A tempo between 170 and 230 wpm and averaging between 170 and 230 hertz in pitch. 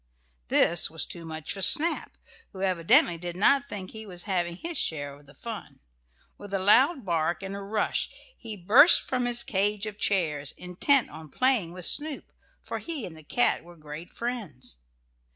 Yes: average, 180 wpm; high, 190 Hz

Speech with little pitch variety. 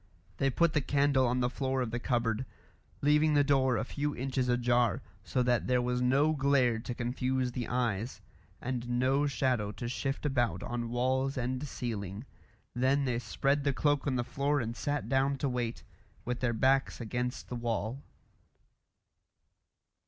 Yes: narrow, 2.2 semitones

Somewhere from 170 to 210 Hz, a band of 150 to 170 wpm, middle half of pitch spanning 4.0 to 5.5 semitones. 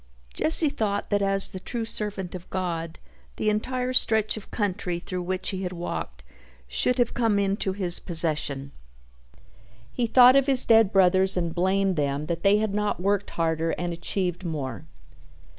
No: high, 190 Hz; average, 165 wpm; average, 3.6 semitones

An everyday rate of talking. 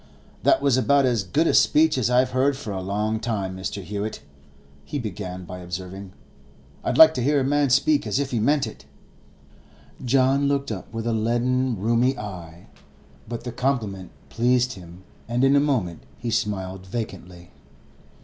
Yes: average, 170 wpm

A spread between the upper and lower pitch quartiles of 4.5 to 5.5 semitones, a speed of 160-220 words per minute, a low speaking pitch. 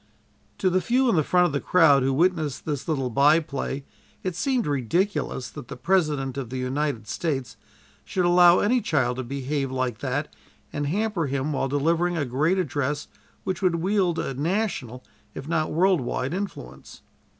No: average, 4.9 semitones; average, 175 wpm; medium, 150 Hz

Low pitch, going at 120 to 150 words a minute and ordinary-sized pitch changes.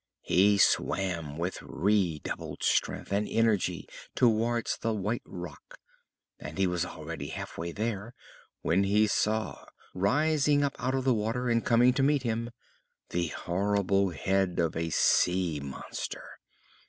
Yes: low, 100 Hz; average, 140 wpm; average, 4.7 semitones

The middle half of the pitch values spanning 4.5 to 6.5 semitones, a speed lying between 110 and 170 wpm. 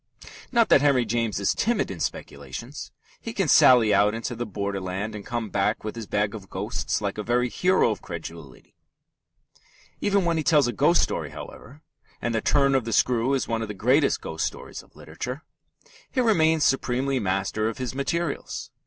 No: average, 5.1 semitones; average, 190 wpm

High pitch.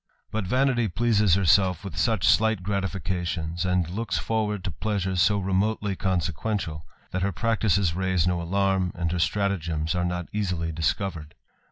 No: very low, 95 Hz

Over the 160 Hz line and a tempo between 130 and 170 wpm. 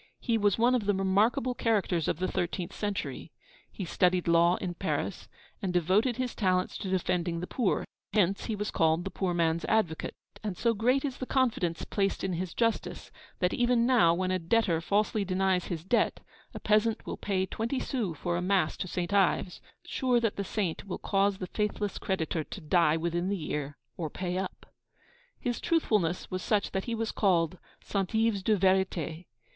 No: high, 190 Hz; average, 190 wpm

